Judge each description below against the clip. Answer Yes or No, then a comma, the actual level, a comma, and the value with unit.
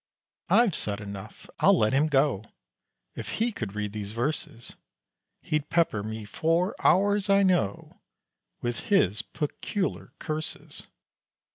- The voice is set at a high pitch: No, medium, 145 Hz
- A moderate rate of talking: No, slow, 125 wpm